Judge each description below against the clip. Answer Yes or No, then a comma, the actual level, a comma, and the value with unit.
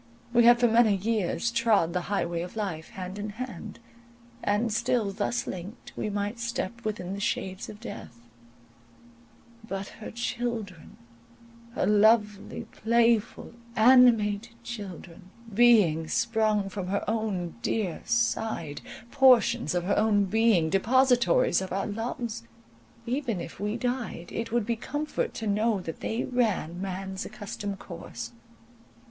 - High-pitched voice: Yes, high, 210 Hz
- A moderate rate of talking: No, slow, 125 wpm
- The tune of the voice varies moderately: Yes, average, 3.7 semitones